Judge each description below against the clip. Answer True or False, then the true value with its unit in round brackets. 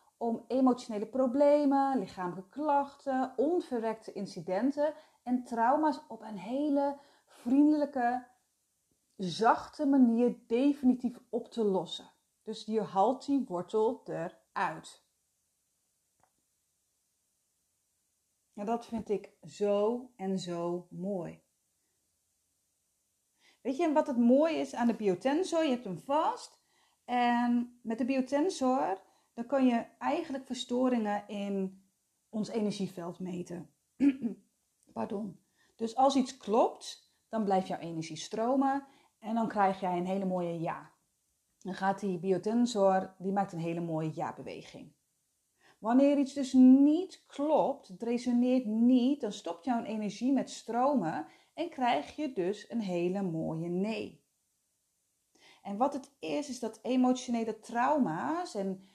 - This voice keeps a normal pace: False (120 wpm)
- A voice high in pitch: True (235 Hz)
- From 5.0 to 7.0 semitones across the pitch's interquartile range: True (5.6 semitones)